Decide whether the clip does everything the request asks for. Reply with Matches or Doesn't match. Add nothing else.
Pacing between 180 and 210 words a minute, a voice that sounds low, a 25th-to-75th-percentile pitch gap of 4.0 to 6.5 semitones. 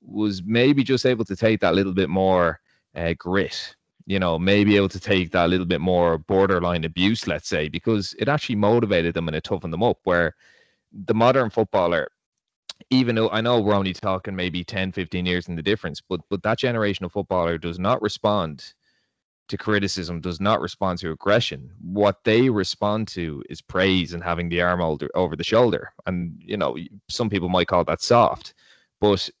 Doesn't match